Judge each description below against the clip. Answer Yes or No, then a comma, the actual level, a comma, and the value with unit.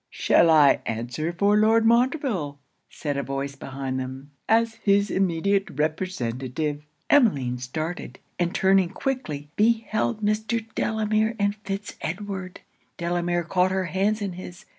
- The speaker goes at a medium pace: No, slow, 130 wpm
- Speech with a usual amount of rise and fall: No, wide, 6.4 semitones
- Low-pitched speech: No, medium, 185 Hz